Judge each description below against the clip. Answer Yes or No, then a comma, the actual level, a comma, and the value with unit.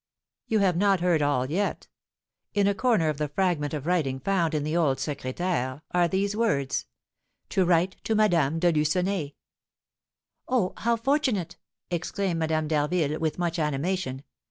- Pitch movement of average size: Yes, average, 4.3 semitones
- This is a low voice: No, medium, 170 Hz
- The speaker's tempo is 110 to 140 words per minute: No, average, 155 wpm